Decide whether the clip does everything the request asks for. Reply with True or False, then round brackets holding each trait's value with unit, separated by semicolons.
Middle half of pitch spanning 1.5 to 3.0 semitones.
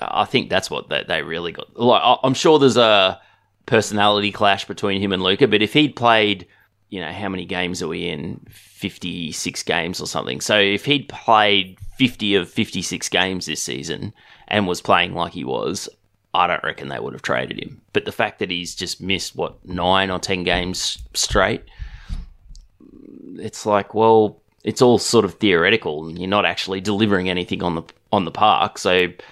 True (2.7 semitones)